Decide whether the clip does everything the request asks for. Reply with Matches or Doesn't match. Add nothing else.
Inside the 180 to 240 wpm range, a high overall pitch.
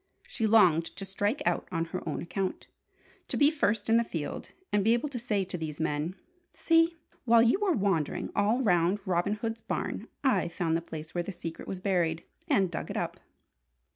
Matches